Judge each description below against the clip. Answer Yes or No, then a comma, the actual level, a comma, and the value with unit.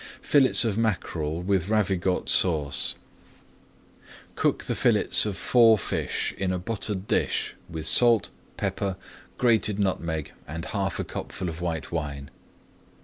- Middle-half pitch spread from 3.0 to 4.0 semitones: No, average, 4.5 semitones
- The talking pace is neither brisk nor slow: No, slow, 130 wpm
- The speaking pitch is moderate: No, very low, 95 Hz